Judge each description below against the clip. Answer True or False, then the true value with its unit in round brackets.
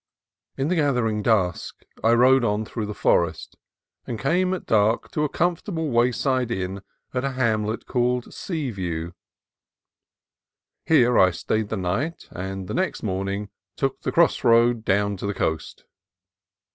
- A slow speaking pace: False (145 wpm)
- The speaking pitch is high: False (115 Hz)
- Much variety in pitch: False (4.8 semitones)